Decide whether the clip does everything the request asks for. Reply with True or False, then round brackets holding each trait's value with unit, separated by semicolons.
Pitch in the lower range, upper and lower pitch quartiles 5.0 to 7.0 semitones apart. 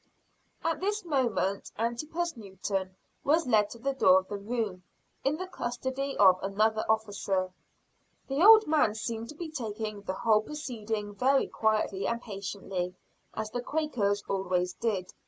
False (220 Hz; 5.4 semitones)